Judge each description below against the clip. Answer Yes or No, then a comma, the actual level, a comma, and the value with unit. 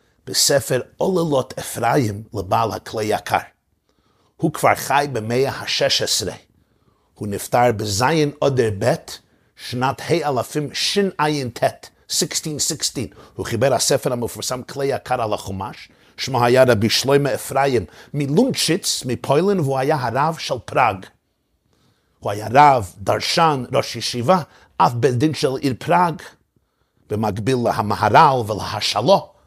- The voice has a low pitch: Yes, low, 130 Hz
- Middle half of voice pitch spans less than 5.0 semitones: Yes, average, 4.5 semitones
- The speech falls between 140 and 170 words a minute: No, average, 115 wpm